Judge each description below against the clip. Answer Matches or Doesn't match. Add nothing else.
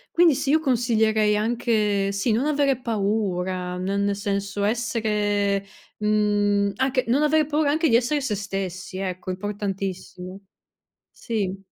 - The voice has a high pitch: Matches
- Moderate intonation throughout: Matches